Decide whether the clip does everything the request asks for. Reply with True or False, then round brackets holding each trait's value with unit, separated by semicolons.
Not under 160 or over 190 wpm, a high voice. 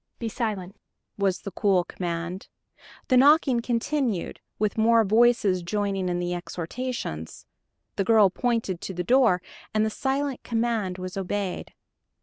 False (135 wpm; 205 Hz)